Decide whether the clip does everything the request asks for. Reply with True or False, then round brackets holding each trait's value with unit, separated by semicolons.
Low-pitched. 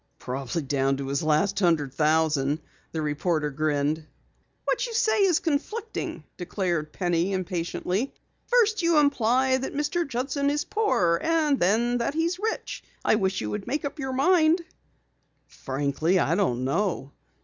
False (195 Hz)